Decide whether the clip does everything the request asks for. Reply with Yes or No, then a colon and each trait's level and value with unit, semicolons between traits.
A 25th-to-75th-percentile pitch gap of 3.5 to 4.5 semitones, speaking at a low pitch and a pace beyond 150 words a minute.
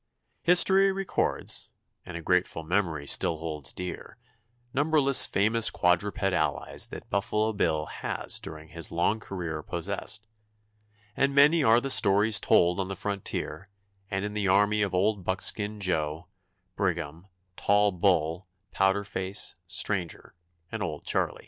No: average, 3.8 semitones; very low, 95 Hz; slow, 135 wpm